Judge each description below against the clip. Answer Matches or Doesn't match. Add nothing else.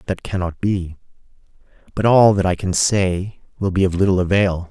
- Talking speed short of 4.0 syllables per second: Doesn't match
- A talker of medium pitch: Doesn't match